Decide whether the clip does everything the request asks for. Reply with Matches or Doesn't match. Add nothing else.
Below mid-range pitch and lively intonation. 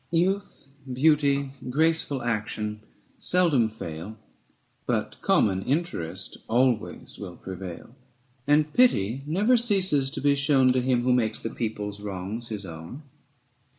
Matches